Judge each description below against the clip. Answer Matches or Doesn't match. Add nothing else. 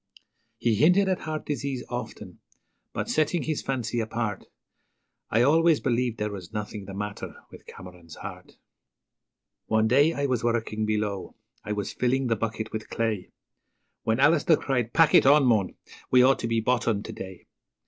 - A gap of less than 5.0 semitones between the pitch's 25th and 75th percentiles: Matches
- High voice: Doesn't match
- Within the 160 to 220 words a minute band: Matches